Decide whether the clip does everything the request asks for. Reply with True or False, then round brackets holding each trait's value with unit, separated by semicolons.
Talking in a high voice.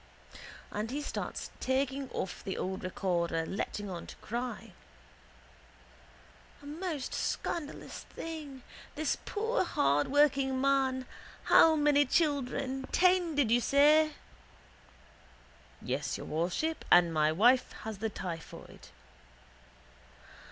True (265 Hz)